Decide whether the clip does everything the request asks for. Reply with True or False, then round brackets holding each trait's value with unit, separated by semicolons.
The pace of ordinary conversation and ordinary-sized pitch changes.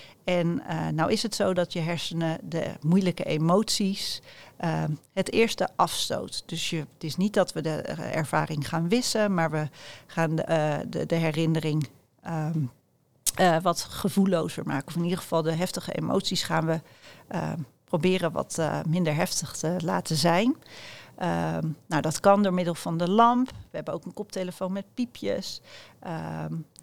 True (170 wpm; 3.1 semitones)